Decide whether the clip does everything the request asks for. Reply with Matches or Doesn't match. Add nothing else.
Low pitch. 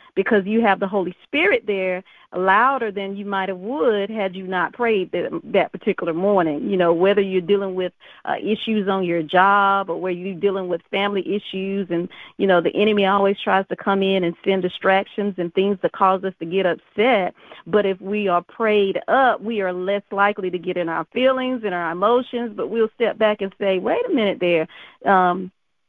Doesn't match